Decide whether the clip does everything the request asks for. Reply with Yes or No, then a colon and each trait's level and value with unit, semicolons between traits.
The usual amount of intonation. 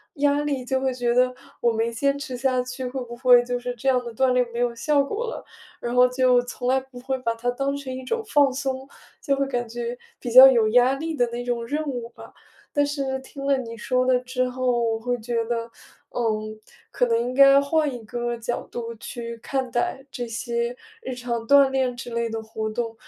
No: narrow, 2.0 semitones